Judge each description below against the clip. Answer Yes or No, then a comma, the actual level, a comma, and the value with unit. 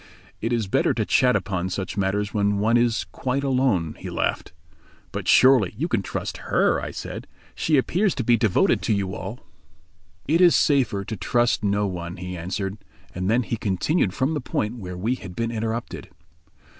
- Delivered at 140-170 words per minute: No, average, 185 wpm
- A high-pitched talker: No, low, 110 Hz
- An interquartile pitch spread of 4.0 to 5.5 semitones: Yes, average, 4.6 semitones